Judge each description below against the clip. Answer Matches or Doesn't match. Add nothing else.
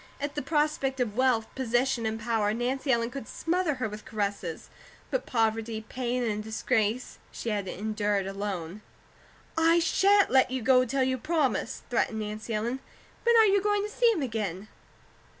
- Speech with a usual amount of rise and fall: Matches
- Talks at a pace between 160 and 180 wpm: Matches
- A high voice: Matches